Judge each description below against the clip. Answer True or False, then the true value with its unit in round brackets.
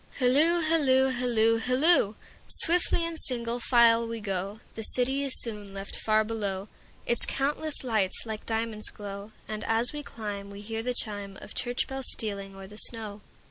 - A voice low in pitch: False (225 Hz)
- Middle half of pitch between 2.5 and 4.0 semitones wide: True (3.6 semitones)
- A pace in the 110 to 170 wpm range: True (145 wpm)